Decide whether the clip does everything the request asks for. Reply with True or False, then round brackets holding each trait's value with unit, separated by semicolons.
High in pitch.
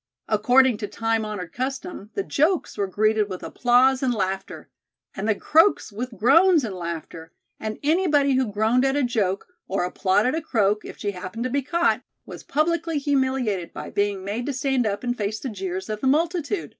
True (235 Hz)